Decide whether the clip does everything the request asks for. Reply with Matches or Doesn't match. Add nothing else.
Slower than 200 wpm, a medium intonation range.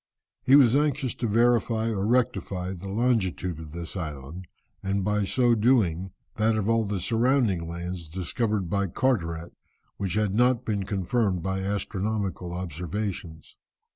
Matches